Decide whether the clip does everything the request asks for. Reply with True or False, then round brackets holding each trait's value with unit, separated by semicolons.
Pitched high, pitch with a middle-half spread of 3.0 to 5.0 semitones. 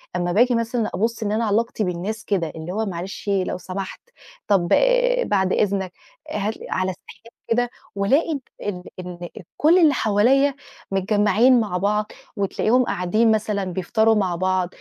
True (205 Hz; 3.3 semitones)